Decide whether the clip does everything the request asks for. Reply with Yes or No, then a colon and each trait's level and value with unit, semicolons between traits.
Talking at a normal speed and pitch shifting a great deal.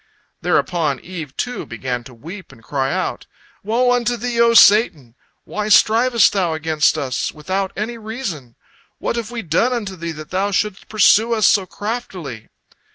Yes: average, 160 wpm; wide, 6.8 semitones